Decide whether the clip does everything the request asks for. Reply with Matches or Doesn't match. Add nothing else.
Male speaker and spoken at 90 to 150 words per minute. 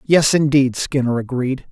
Matches